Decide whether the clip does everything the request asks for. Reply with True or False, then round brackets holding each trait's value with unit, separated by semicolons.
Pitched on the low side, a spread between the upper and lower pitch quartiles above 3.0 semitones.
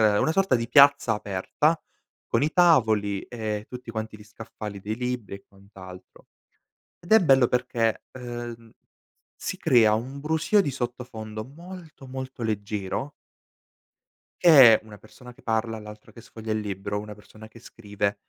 True (115 Hz; 3.7 semitones)